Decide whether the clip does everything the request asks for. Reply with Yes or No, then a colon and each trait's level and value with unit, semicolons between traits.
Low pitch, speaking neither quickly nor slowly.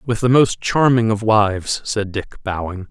Yes: low, 110 Hz; average, 185 wpm